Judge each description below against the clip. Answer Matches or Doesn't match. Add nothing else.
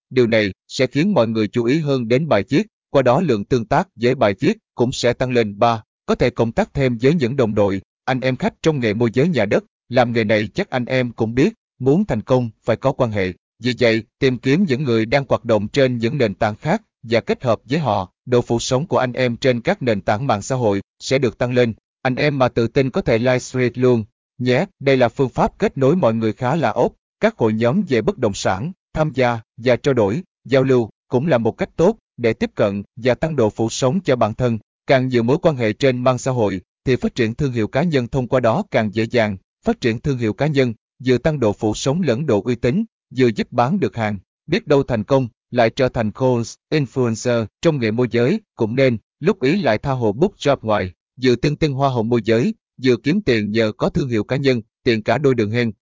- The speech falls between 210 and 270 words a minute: Matches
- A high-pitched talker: Doesn't match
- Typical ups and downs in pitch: Matches